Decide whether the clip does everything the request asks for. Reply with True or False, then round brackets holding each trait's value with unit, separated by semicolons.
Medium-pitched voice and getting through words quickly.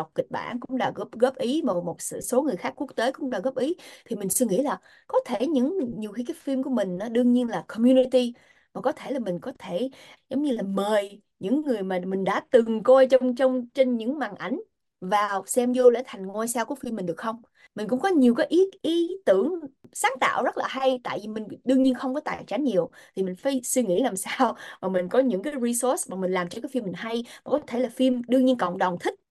False (255 Hz; 260 wpm)